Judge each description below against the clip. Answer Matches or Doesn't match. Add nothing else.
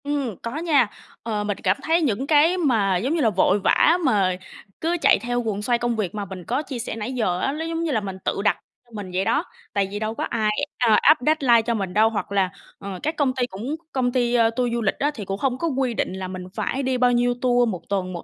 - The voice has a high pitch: Matches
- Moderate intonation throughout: Matches